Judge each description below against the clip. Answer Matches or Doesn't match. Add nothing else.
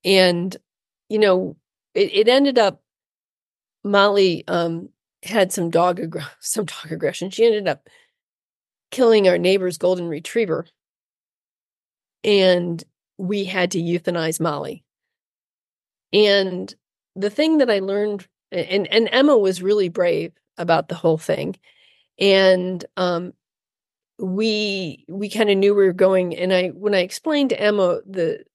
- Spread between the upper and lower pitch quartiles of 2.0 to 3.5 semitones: Matches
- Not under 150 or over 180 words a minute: Doesn't match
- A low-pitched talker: Doesn't match